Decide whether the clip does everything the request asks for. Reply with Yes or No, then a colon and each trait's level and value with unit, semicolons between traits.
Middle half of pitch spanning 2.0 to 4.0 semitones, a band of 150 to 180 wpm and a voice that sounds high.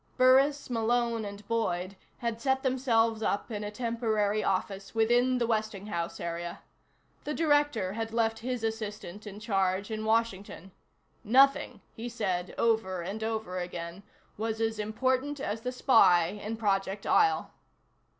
No: average, 3.1 semitones; average, 140 wpm; high, 220 Hz